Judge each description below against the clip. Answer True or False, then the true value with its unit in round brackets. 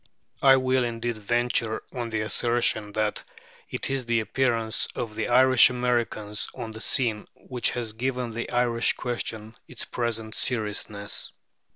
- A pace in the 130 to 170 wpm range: True (145 wpm)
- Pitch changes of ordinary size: False (2.1 semitones)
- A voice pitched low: True (115 Hz)